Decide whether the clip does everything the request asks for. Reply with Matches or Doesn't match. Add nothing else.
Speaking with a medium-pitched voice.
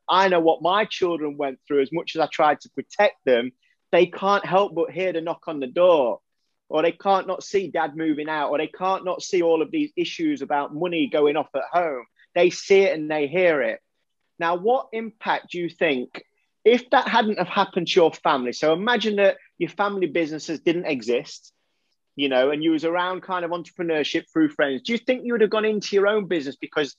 Matches